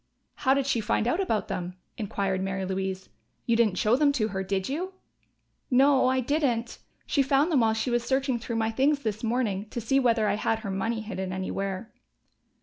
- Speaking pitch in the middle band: No, high, 230 Hz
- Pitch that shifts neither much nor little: Yes, average, 5.0 semitones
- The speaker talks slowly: No, average, 200 wpm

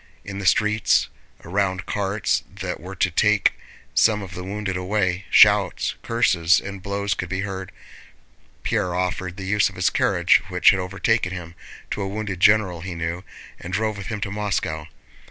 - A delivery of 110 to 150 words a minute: No, average, 175 wpm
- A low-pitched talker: Yes, very low, 95 Hz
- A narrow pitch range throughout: Yes, narrow, 2.2 semitones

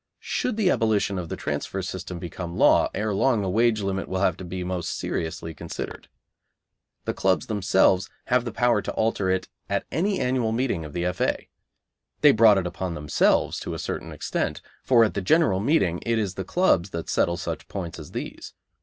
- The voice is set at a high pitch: No, very low, 95 Hz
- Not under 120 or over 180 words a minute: No, average, 195 wpm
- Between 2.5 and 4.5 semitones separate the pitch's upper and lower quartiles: Yes, average, 4.2 semitones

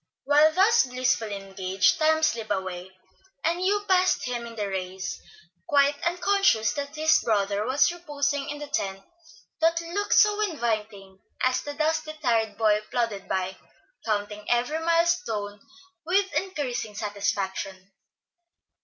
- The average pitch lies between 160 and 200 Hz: No, very high, 250 Hz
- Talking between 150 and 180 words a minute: No, slow, 135 wpm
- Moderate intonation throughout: No, wide, 7.6 semitones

